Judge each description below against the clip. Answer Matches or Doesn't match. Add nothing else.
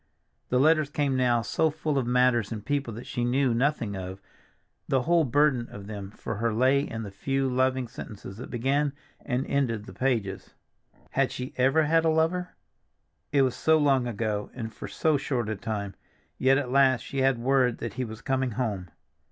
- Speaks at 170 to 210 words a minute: Matches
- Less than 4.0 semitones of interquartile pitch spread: Matches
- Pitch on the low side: Matches